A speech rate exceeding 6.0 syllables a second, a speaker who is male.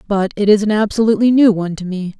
No: 7.0 syllables/s; female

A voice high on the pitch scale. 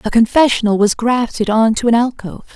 Yes: high, 230 Hz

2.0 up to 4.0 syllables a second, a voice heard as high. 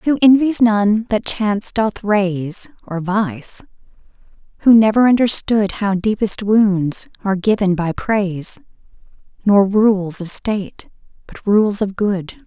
Yes: 3.9 syllables/s; high, 205 Hz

